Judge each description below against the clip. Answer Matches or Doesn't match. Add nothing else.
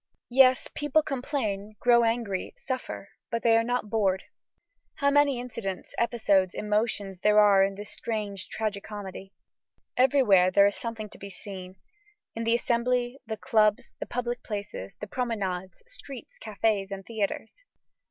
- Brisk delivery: Doesn't match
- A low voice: Doesn't match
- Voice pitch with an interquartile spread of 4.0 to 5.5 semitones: Doesn't match